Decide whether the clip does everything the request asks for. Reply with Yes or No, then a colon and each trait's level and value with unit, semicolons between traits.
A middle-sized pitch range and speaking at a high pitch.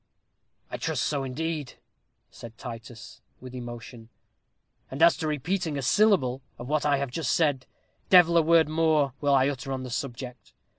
No: average, 4.0 semitones; medium, 140 Hz